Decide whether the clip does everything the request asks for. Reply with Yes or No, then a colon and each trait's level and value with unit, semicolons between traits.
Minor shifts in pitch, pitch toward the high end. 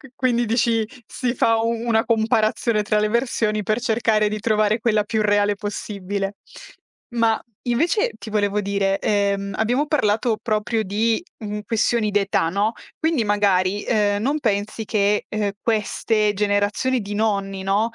Yes: narrow, 2.0 semitones; high, 215 Hz